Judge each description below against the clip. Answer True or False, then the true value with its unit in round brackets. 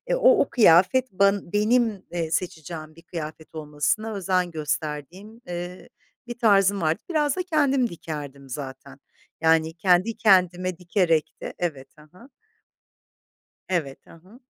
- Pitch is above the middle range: False (180 Hz)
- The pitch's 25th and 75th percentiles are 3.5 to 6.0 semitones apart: True (5.0 semitones)